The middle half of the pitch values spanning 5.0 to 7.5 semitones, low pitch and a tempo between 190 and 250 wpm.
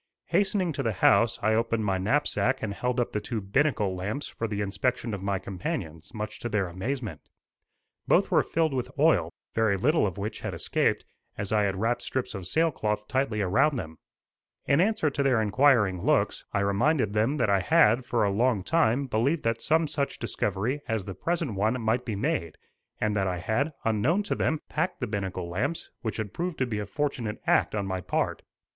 Yes: wide, 5.5 semitones; low, 110 Hz; average, 200 wpm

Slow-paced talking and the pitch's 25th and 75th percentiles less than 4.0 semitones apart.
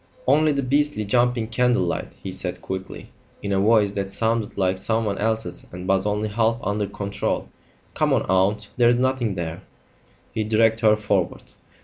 No: average, 165 wpm; average, 2.8 semitones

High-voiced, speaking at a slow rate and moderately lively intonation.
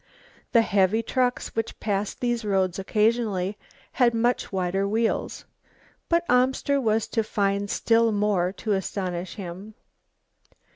Yes: high, 210 Hz; slow, 125 wpm; average, 3.1 semitones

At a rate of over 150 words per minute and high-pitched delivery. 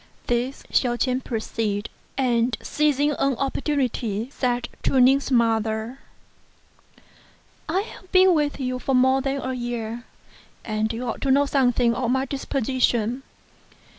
No: slow, 135 wpm; very high, 255 Hz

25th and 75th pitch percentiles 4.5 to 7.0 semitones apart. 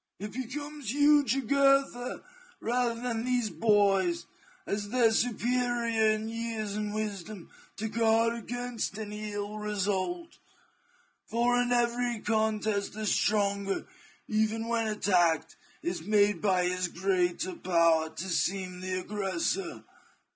No: average, 3.3 semitones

